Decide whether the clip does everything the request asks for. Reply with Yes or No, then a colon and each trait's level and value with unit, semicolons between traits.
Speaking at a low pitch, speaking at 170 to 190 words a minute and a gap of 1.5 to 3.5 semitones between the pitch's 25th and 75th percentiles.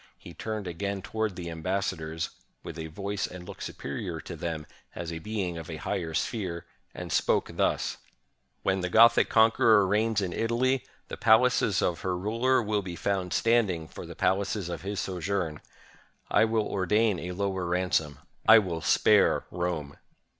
No: very low, 95 Hz; average, 175 wpm; average, 4.0 semitones